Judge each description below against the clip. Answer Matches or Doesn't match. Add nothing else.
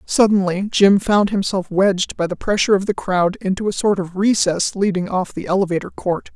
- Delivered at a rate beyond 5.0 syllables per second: Matches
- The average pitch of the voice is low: Doesn't match